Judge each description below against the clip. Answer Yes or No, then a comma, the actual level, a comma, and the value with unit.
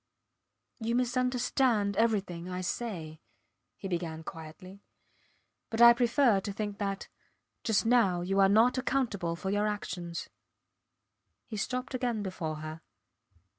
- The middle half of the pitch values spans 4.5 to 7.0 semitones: Yes, average, 4.9 semitones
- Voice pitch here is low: No, high, 205 Hz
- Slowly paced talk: Yes, slow, 125 wpm